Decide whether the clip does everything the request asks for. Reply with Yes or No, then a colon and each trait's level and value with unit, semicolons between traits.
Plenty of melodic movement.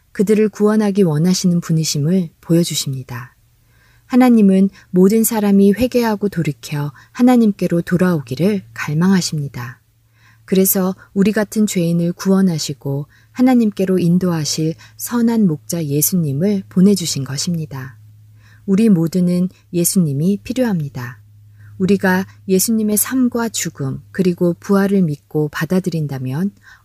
Yes: wide, 5.7 semitones